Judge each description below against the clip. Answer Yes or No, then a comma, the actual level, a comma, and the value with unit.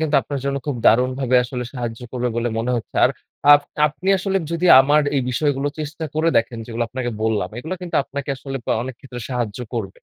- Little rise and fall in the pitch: No, average, 3.4 semitones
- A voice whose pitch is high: No, low, 130 Hz